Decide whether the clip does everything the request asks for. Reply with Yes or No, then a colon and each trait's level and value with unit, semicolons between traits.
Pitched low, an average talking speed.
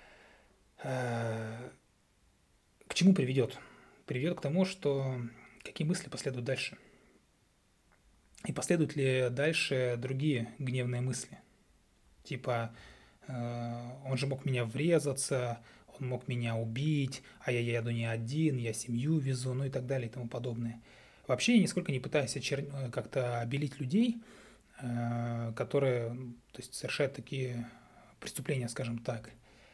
Yes: low, 130 Hz; average, 120 wpm